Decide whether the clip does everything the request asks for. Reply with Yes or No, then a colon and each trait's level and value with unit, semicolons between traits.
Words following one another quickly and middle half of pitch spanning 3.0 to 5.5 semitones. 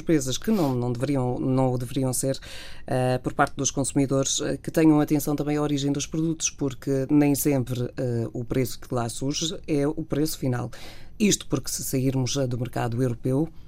No: fast, 190 wpm; narrow, 2.6 semitones